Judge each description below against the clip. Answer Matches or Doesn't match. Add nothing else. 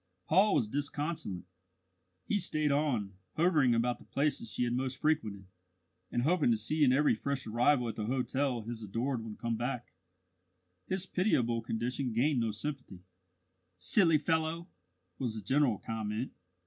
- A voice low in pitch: Matches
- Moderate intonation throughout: Matches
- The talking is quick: Doesn't match